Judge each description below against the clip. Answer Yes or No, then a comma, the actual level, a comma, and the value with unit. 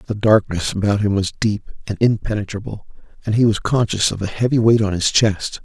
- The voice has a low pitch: Yes, low, 105 Hz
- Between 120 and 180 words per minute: No, average, 200 wpm